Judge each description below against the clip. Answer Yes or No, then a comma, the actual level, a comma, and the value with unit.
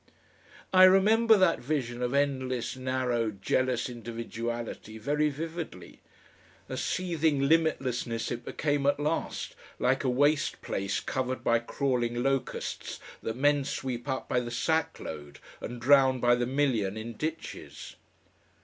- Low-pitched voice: Yes, low, 130 Hz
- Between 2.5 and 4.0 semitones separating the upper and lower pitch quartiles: Yes, average, 3.6 semitones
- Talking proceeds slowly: Yes, slow, 130 wpm